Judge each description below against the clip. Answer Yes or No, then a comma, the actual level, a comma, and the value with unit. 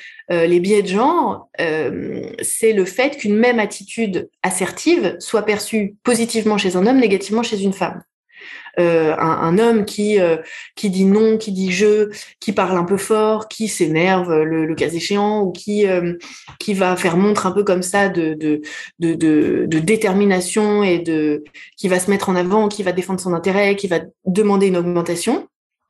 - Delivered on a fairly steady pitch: No, average, 3.4 semitones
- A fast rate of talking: No, average, 185 wpm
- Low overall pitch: No, high, 195 Hz